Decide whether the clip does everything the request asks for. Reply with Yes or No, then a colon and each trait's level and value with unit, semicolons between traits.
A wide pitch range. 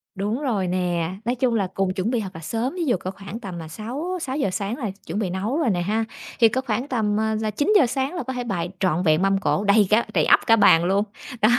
No: average, 4.6 semitones